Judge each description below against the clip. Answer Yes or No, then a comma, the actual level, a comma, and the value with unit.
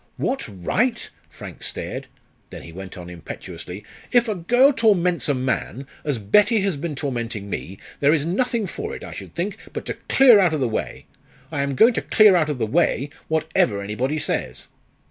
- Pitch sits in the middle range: Yes, medium, 150 Hz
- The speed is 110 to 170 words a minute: No, average, 190 wpm